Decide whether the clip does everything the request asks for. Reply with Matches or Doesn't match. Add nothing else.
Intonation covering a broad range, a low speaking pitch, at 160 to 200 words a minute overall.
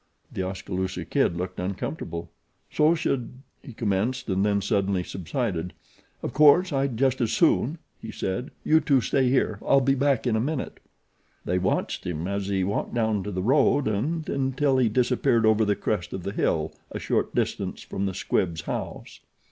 Matches